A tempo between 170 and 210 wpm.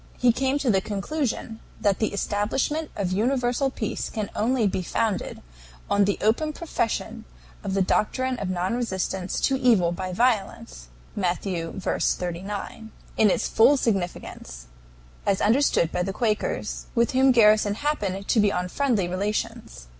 No: average, 150 wpm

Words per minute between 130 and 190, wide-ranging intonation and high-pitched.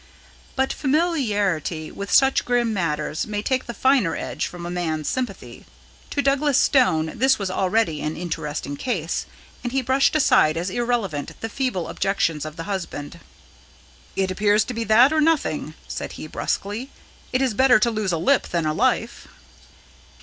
Yes: average, 165 wpm; wide, 7.7 semitones; high, 210 Hz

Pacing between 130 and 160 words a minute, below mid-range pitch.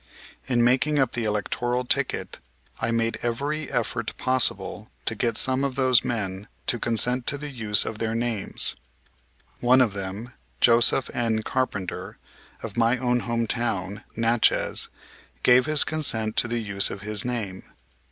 Yes: average, 150 wpm; low, 120 Hz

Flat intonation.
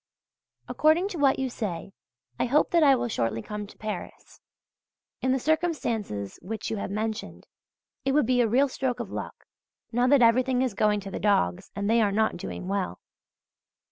No: average, 4.6 semitones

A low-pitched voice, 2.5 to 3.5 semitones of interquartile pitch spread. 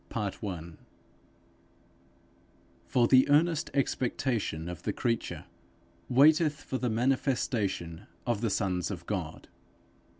No: low, 120 Hz; wide, 5.6 semitones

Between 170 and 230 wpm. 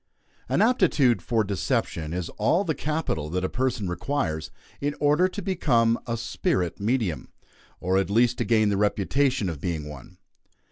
No: average, 160 wpm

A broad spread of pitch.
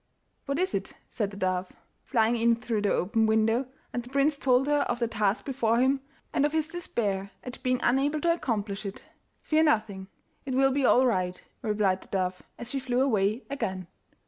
No: average, 4.8 semitones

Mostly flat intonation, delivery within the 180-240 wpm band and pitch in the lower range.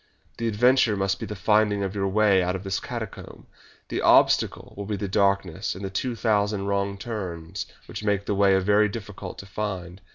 Yes: narrow, 1.5 semitones; average, 200 wpm; low, 100 Hz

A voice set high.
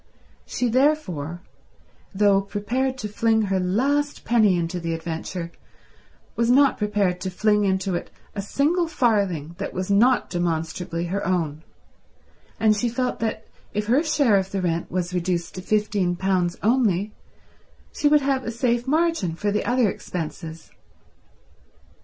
Yes: high, 205 Hz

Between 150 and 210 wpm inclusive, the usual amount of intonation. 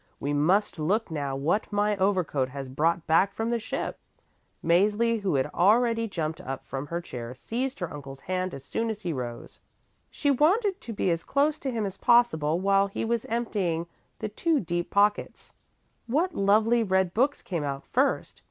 No: average, 180 wpm; wide, 6.2 semitones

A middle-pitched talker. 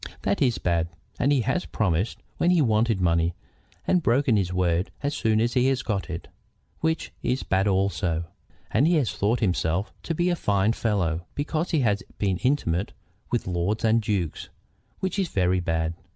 No: low, 105 Hz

